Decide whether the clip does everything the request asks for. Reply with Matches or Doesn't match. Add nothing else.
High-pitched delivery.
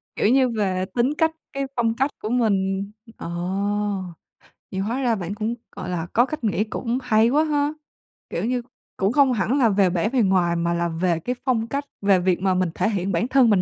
Matches